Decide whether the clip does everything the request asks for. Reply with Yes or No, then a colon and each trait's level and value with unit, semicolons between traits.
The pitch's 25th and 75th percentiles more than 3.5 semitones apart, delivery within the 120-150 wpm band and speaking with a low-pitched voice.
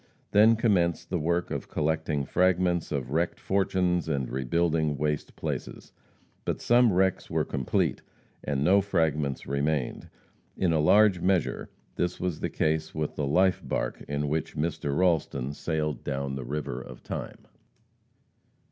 Yes: average, 3.9 semitones; average, 145 wpm; very low, 80 Hz